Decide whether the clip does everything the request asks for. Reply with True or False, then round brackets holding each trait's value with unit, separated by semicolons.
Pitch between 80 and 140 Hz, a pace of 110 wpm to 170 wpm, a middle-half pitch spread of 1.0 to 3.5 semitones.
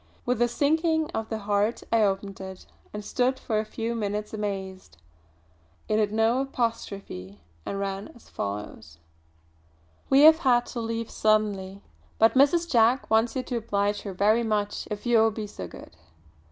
False (220 Hz; 165 wpm; 3.1 semitones)